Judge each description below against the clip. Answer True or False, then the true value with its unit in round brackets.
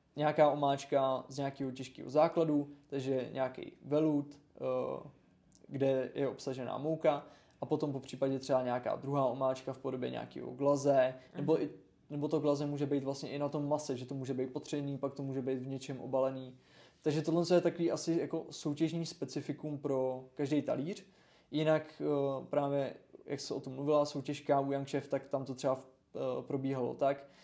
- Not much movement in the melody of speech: True (2.0 semitones)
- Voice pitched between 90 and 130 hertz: False (140 Hz)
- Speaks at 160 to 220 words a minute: True (165 wpm)